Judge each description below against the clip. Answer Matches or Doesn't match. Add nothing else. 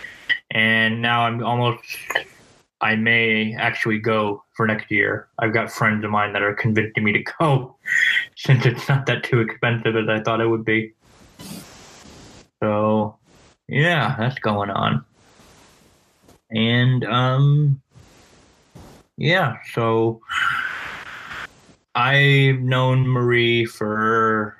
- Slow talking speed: Matches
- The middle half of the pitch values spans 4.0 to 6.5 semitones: Doesn't match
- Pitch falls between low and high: Doesn't match